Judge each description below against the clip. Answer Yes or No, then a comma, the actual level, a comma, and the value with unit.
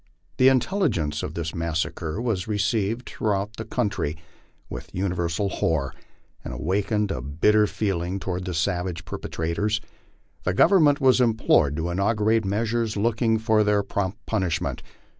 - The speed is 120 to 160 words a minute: Yes, average, 140 wpm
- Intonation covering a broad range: No, average, 4.5 semitones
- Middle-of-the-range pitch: No, low, 100 Hz